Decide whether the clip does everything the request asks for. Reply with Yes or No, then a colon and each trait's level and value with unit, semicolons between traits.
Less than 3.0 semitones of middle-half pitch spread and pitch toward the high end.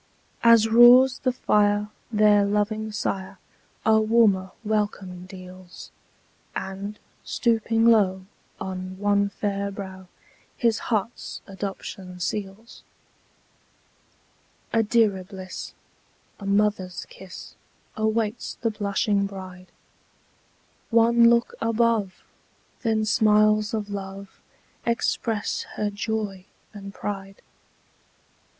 Yes: narrow, 2.4 semitones; high, 205 Hz